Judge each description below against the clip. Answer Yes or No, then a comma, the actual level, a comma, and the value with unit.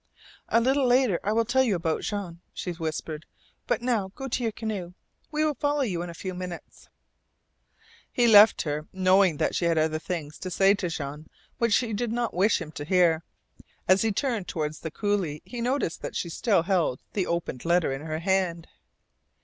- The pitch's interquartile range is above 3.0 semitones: Yes, wide, 5.4 semitones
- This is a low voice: No, medium, 185 Hz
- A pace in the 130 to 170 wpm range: No, average, 200 wpm